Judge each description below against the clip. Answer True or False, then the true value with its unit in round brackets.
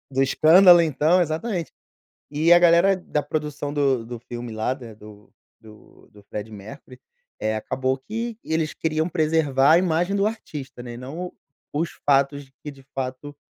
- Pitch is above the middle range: False (145 Hz)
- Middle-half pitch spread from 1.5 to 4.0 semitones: False (4.6 semitones)